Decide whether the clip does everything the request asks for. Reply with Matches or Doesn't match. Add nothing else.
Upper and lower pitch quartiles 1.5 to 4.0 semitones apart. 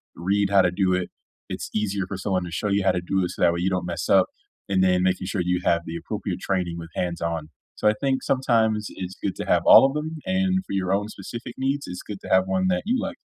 Matches